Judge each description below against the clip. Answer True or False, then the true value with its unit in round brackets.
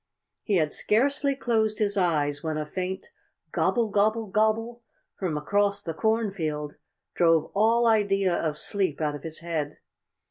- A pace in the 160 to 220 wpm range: False (145 wpm)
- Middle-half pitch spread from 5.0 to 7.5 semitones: True (5.4 semitones)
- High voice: True (195 Hz)